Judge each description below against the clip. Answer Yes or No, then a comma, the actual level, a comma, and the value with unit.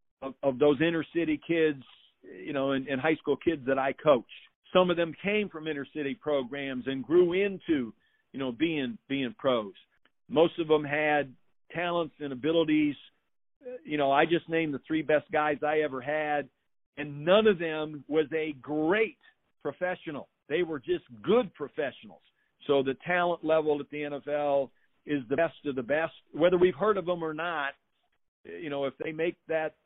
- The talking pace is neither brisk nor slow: Yes, average, 180 wpm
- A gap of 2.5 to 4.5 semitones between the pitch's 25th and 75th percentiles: Yes, average, 3.1 semitones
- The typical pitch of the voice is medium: Yes, medium, 155 Hz